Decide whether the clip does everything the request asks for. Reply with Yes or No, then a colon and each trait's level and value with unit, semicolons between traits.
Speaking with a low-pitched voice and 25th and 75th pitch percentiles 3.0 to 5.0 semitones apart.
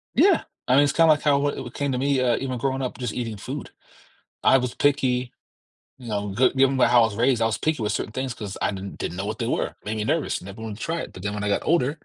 Yes: low, 125 Hz; average, 4.1 semitones